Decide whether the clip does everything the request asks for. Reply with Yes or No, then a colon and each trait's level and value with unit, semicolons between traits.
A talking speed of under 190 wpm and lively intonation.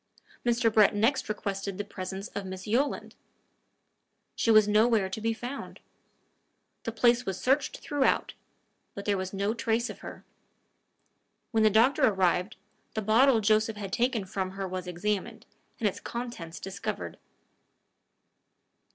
No: average, 140 wpm; average, 3.3 semitones